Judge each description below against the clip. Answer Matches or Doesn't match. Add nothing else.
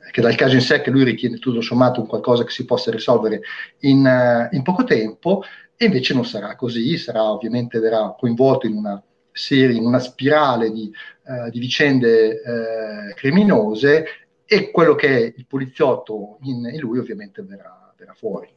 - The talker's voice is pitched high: Doesn't match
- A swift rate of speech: Matches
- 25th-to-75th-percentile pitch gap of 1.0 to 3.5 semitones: Matches